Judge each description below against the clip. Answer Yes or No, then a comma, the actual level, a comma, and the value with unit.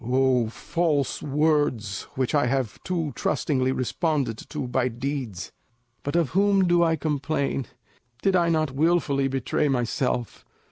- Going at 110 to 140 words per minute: Yes, slow, 135 wpm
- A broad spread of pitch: No, average, 3.8 semitones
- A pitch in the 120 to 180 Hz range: Yes, medium, 140 Hz